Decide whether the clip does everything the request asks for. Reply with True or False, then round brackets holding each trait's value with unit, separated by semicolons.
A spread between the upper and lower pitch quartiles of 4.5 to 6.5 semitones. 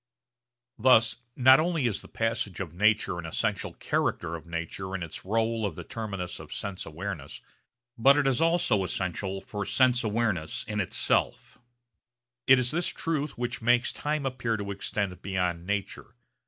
True (4.8 semitones)